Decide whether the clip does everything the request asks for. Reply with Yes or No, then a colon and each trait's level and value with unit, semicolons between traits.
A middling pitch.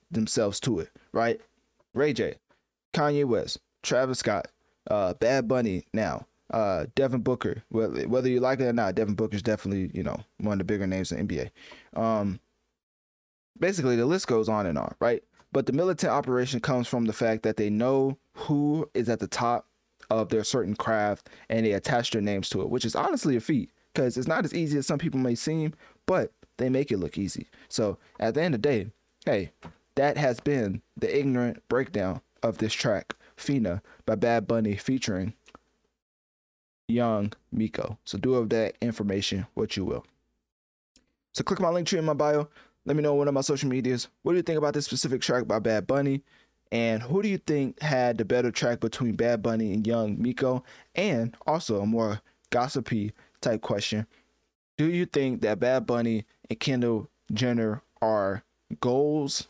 No: low, 120 Hz